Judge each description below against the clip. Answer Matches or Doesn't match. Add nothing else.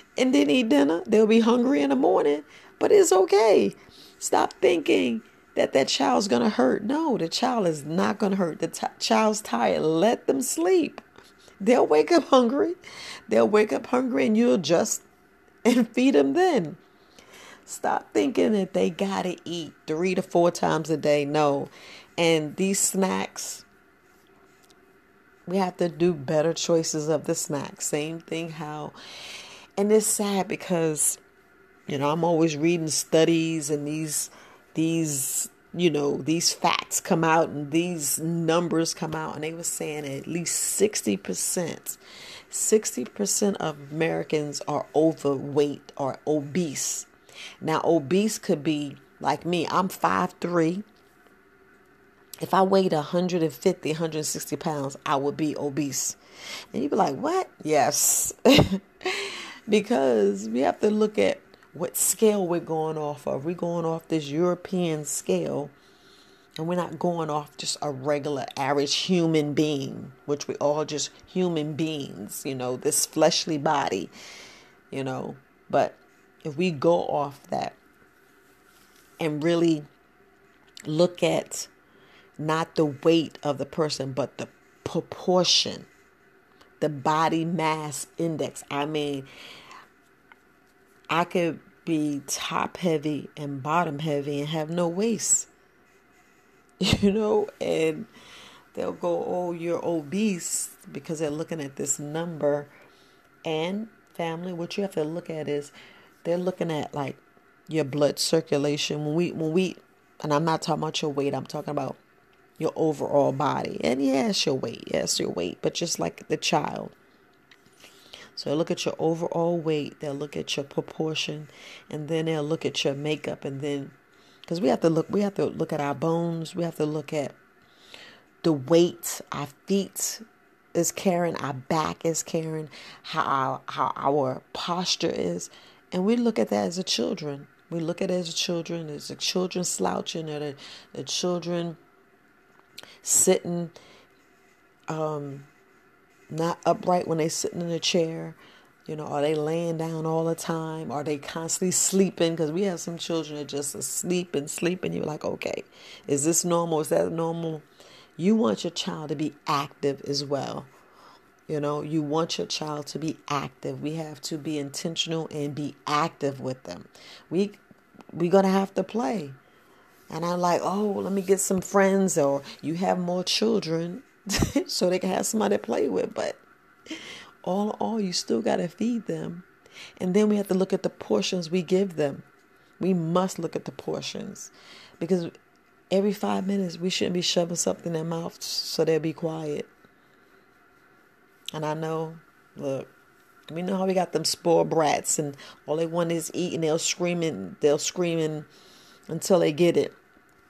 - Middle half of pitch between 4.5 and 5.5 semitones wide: Doesn't match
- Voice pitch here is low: Doesn't match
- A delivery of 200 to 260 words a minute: Doesn't match